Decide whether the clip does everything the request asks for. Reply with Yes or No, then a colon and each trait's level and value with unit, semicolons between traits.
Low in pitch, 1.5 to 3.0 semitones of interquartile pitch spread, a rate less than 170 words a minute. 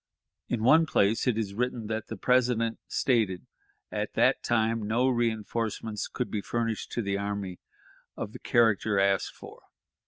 Yes: low, 110 Hz; narrow, 2.6 semitones; average, 155 wpm